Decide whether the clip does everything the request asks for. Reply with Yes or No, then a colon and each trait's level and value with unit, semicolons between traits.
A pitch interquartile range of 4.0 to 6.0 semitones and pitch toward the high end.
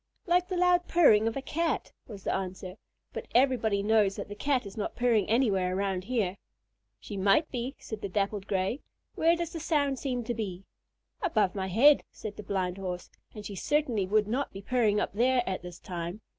Yes: average, 5.3 semitones; high, 215 Hz